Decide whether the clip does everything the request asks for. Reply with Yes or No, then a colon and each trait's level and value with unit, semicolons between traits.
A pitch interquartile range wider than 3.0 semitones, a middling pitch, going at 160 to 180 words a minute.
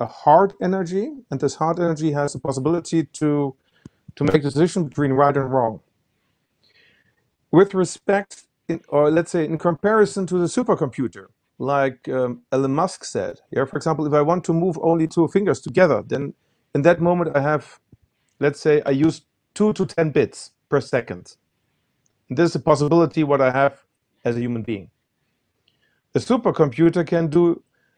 Yes: average, 3.7 semitones; medium, 155 Hz; average, 170 wpm